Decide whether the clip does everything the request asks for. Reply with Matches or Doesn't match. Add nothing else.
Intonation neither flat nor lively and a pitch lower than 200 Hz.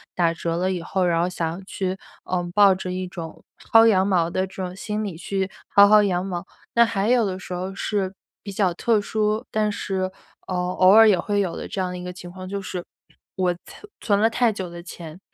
Doesn't match